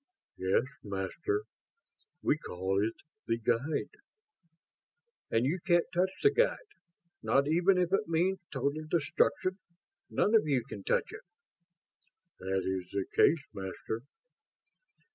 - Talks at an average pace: No, slow, 125 wpm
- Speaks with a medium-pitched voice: Yes, medium, 145 Hz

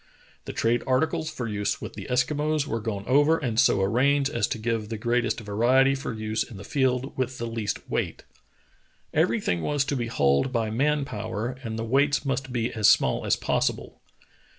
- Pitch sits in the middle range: No, low, 120 Hz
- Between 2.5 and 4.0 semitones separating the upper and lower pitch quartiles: Yes, average, 3.5 semitones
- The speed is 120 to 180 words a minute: No, average, 200 wpm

